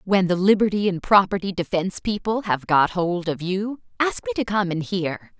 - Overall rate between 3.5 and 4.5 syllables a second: No, 5.1 syllables/s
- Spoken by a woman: Yes, female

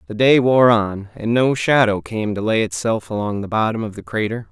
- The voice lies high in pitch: No, low, 110 Hz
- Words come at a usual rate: No, fast, 225 wpm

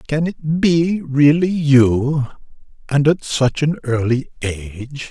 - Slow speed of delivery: Yes, slow, 130 wpm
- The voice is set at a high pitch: No, medium, 145 Hz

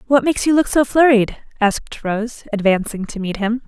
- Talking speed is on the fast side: No, average, 195 wpm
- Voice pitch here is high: Yes, high, 230 Hz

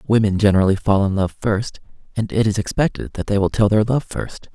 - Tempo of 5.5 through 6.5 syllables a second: Yes, 5.8 syllables/s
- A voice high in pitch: No, low, 105 Hz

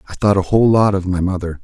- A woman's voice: No, male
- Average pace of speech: No, fast, 295 wpm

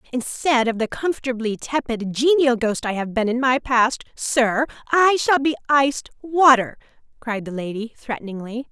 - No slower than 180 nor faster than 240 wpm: No, average, 160 wpm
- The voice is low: No, very high, 250 Hz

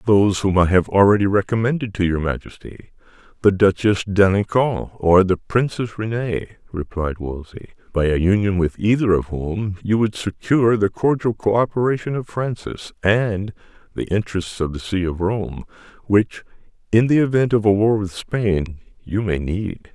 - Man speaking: Yes, male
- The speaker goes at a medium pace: Yes, average, 160 wpm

